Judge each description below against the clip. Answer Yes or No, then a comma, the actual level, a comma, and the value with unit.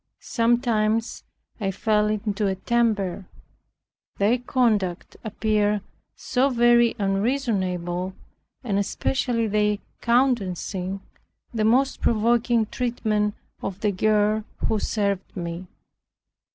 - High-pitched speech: Yes, high, 215 Hz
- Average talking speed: No, slow, 95 wpm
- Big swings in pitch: No, average, 3.1 semitones